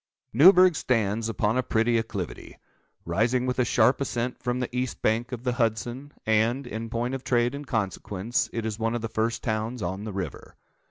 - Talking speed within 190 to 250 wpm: Yes, average, 195 wpm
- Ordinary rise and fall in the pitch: No, narrow, 2.3 semitones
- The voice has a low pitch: Yes, low, 115 Hz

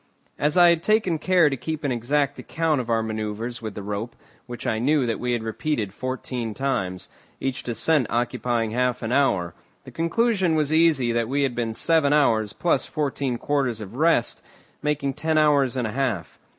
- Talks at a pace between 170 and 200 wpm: Yes, average, 190 wpm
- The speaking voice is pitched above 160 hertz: No, low, 130 Hz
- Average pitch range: Yes, average, 4.7 semitones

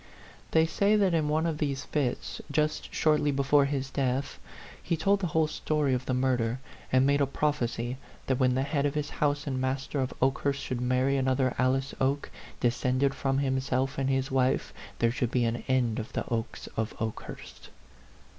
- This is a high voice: No, low, 135 Hz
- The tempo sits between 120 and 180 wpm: No, average, 195 wpm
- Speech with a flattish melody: Yes, narrow, 2.3 semitones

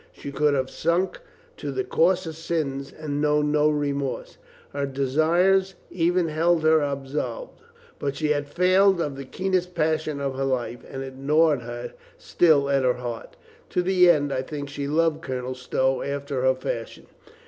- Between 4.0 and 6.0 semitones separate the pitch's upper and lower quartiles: No, average, 3.5 semitones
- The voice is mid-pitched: Yes, medium, 150 Hz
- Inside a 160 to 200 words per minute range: Yes, average, 165 wpm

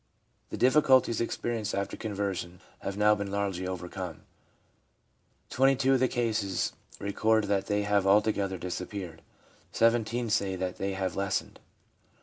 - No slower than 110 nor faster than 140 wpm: Yes, slow, 135 wpm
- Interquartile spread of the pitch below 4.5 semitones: Yes, average, 2.8 semitones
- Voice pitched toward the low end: Yes, low, 100 Hz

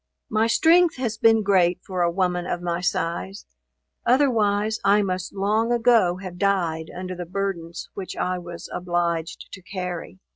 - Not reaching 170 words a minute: Yes, average, 155 wpm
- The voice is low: No, medium, 185 Hz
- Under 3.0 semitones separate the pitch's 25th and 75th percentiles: No, average, 3.4 semitones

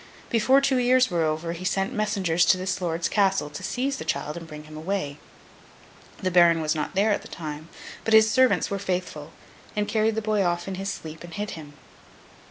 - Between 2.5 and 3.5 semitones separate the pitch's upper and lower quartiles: No, average, 4.7 semitones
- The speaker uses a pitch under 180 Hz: No, medium, 185 Hz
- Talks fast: Yes, fast, 210 wpm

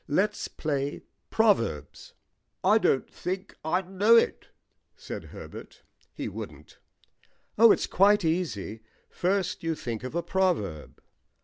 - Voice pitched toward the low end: No, medium, 180 Hz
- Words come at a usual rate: No, slow, 120 wpm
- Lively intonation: Yes, wide, 6.3 semitones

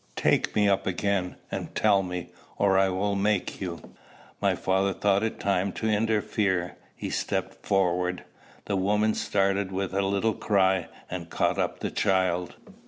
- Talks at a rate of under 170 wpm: Yes, average, 160 wpm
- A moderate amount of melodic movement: No, narrow, 1.5 semitones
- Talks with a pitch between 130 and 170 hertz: No, very low, 95 Hz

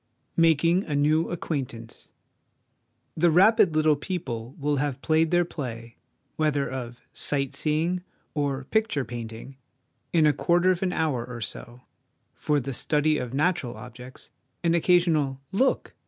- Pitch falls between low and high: Yes, medium, 150 Hz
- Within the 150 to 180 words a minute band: No, average, 140 wpm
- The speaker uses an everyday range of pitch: Yes, average, 4.5 semitones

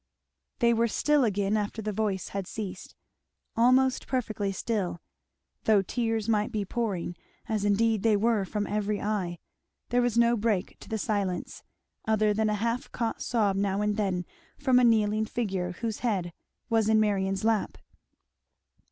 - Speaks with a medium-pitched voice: No, high, 215 Hz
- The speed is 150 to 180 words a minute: Yes, average, 160 wpm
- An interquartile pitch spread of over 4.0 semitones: No, narrow, 2.4 semitones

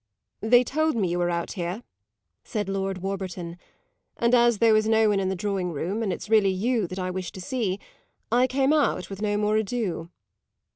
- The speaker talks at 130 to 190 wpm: No, average, 200 wpm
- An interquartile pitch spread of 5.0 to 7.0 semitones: No, average, 3.8 semitones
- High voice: Yes, high, 205 Hz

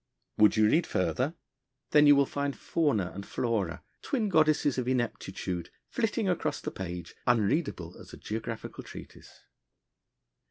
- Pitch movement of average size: No, wide, 6.7 semitones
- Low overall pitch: Yes, low, 120 Hz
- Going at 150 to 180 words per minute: No, slow, 135 wpm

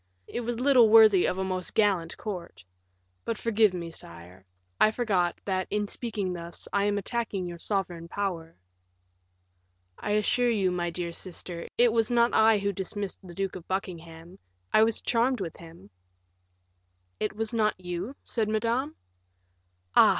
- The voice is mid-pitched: No, high, 195 Hz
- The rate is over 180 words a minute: No, average, 155 wpm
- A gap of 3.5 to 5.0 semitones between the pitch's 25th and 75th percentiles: Yes, average, 4.1 semitones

